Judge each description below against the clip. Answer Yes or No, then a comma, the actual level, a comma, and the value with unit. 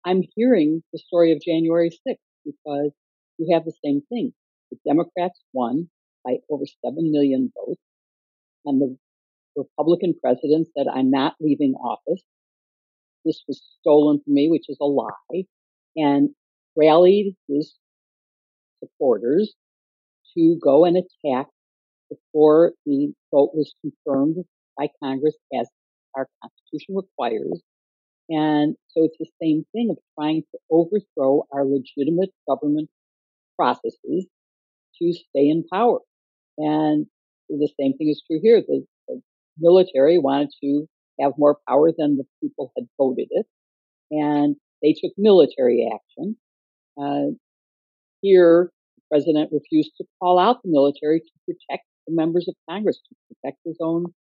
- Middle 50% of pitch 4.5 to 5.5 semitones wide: No, average, 4.0 semitones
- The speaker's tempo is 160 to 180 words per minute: No, slow, 135 wpm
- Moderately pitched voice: Yes, medium, 155 Hz